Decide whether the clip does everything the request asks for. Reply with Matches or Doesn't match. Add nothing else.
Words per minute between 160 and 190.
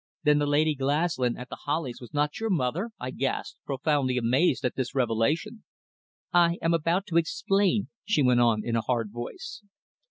Matches